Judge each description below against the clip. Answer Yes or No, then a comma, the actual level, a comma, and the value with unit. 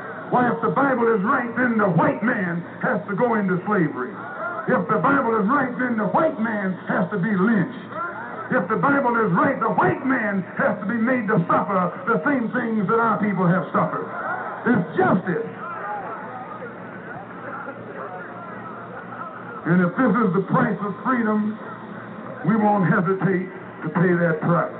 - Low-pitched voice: No, high, 210 Hz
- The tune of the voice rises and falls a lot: No, average, 3.3 semitones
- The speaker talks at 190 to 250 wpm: No, average, 165 wpm